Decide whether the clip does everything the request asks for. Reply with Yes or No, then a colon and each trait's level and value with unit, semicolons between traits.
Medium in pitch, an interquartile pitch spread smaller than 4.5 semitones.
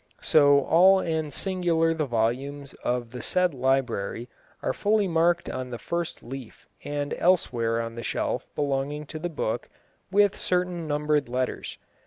No: medium, 145 Hz; average, 5.2 semitones